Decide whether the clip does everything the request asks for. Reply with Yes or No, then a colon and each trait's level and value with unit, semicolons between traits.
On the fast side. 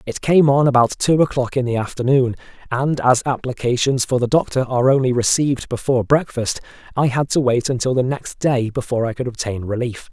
No: average, 195 wpm